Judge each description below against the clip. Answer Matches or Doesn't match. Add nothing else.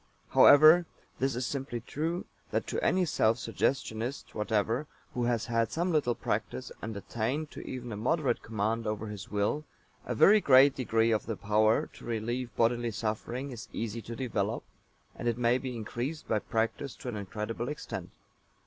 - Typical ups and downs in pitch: Matches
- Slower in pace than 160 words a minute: Doesn't match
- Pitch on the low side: Matches